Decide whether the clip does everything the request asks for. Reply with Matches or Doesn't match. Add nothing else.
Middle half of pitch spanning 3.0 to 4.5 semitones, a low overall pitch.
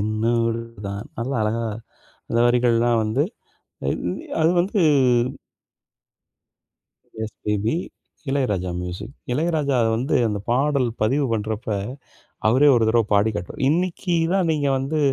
Doesn't match